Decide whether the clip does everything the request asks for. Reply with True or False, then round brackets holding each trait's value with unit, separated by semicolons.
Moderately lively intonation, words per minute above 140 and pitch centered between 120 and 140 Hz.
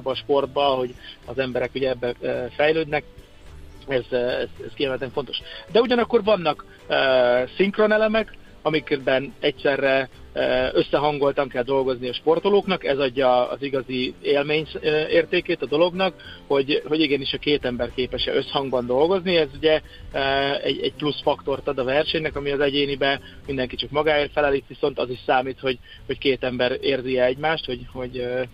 True (3.0 semitones; 150 wpm; 135 Hz)